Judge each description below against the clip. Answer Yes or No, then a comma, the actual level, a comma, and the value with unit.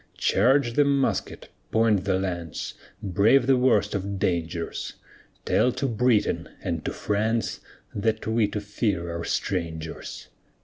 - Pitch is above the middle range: No, low, 105 Hz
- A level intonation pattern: No, average, 4.1 semitones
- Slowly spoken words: Yes, slow, 130 wpm